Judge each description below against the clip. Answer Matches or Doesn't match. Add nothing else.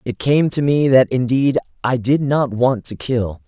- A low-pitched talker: Matches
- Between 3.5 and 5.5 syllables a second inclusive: Matches